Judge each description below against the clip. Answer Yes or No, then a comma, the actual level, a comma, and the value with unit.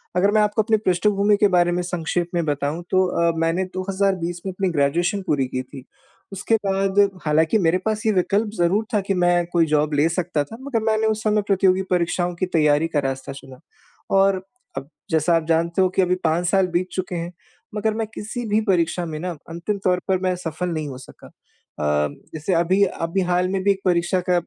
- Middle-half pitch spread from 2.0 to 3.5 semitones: Yes, average, 3.1 semitones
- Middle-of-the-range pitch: Yes, medium, 180 Hz